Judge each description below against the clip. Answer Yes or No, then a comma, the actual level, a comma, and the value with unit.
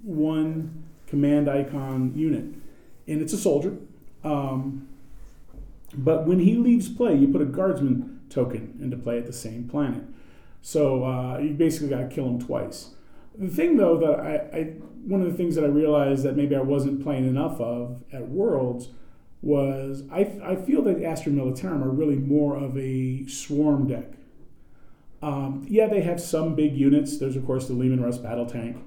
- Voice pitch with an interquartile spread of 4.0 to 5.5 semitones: No, average, 3.3 semitones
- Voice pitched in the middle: Yes, medium, 145 Hz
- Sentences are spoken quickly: No, average, 175 wpm